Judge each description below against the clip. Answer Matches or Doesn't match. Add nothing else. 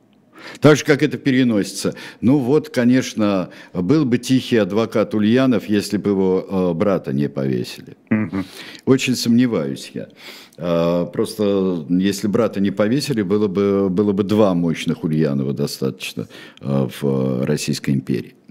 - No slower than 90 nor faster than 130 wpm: Matches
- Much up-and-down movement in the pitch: Matches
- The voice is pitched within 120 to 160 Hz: Doesn't match